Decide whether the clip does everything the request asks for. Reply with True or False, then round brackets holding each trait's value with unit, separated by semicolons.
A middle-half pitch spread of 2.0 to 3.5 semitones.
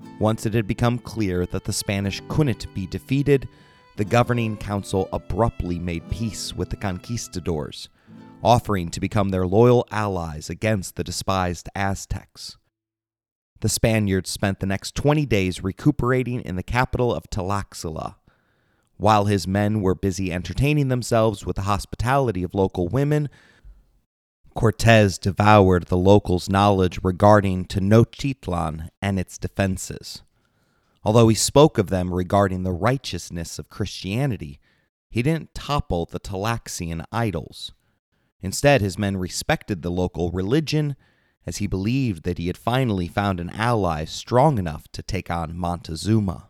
False (4.2 semitones)